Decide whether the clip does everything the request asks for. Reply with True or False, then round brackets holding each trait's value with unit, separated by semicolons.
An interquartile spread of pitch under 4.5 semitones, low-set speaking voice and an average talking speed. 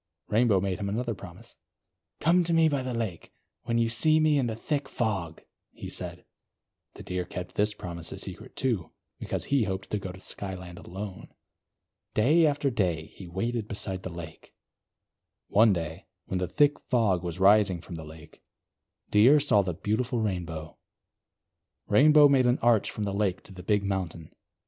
False (5.1 semitones; 105 Hz; 175 wpm)